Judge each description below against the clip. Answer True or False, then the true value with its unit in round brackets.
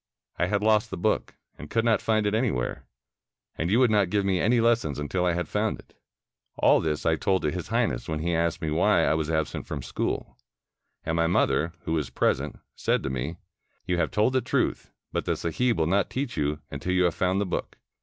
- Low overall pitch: True (90 Hz)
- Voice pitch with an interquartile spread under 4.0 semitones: False (5.0 semitones)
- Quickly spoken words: True (225 wpm)